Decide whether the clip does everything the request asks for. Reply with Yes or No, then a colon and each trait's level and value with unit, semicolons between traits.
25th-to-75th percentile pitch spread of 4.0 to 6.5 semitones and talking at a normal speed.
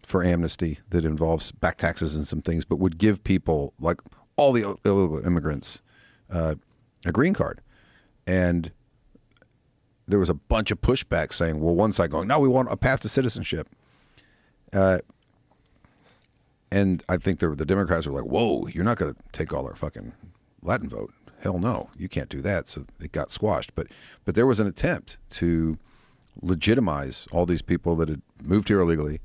Yes: average, 4.7 semitones; average, 180 wpm